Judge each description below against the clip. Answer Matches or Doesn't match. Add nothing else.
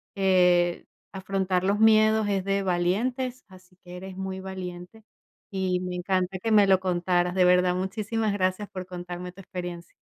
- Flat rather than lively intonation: Matches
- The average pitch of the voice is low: Doesn't match